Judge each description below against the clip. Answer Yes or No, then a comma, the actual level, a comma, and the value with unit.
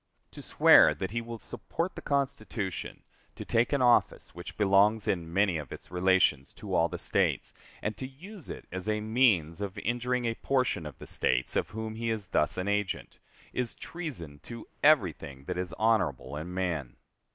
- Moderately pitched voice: No, low, 105 Hz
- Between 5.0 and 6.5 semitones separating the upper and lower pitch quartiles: Yes, average, 5.3 semitones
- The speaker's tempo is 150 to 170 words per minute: No, average, 185 wpm